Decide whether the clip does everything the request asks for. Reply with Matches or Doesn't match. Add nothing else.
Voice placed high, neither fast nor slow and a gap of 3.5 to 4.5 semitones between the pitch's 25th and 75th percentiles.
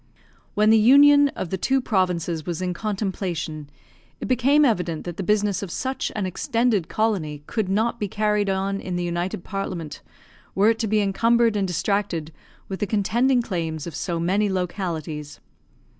Matches